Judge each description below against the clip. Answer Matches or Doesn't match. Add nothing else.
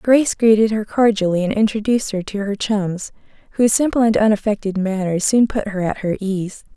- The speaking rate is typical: Matches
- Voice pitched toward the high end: Matches